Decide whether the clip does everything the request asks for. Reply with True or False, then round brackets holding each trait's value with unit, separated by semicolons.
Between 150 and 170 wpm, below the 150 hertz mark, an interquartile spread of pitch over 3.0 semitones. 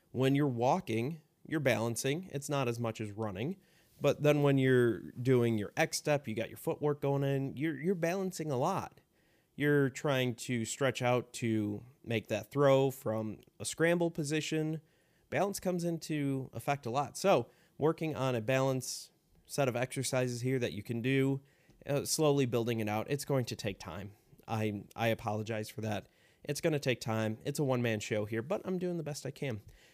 False (190 wpm; 135 Hz; 4.9 semitones)